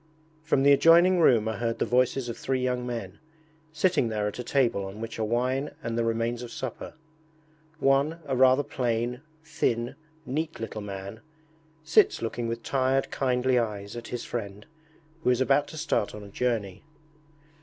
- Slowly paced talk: No, average, 175 wpm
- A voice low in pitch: Yes, low, 125 Hz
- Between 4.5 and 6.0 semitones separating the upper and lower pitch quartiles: No, average, 3.1 semitones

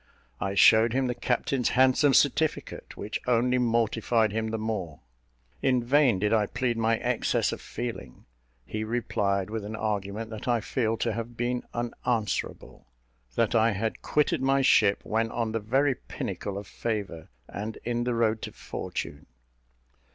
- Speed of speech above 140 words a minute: Yes, average, 160 wpm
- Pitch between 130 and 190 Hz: No, low, 115 Hz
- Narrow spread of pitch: Yes, narrow, 2.2 semitones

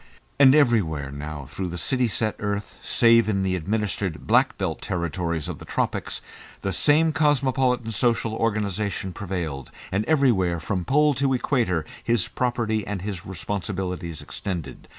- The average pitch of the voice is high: No, low, 100 Hz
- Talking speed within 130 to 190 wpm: Yes, average, 145 wpm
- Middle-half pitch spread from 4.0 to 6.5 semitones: Yes, wide, 5.4 semitones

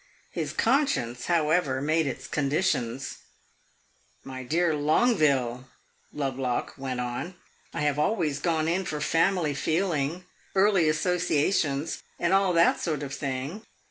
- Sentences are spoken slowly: Yes, slow, 120 wpm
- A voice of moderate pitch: Yes, medium, 150 Hz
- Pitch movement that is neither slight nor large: Yes, average, 4.5 semitones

